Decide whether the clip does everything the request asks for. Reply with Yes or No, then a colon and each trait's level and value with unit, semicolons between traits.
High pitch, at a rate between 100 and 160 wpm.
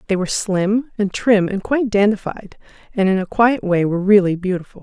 No: high, 200 Hz; average, 200 wpm